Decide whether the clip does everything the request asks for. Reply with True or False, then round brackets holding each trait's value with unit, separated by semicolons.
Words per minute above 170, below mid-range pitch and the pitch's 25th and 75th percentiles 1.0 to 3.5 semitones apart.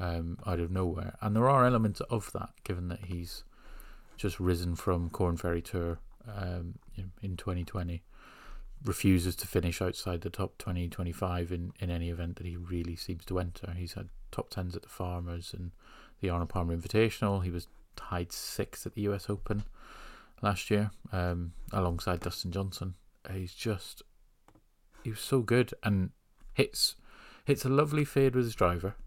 True (180 wpm; 90 Hz; 3.0 semitones)